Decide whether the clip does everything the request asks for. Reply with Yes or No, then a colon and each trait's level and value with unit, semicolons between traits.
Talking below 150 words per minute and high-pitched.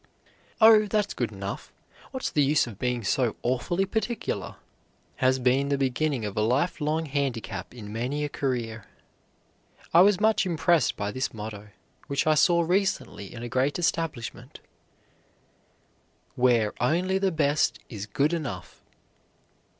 No: average, 140 wpm; medium, 140 Hz